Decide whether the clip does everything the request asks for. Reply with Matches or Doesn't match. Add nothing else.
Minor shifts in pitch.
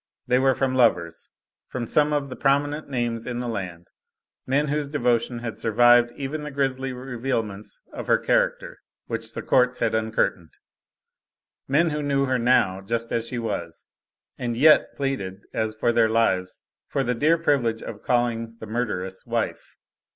Doesn't match